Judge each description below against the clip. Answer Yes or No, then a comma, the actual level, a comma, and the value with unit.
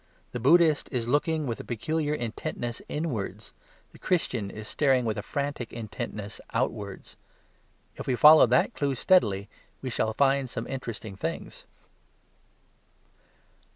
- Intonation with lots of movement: No, average, 4.7 semitones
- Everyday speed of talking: No, slow, 130 wpm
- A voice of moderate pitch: No, low, 125 Hz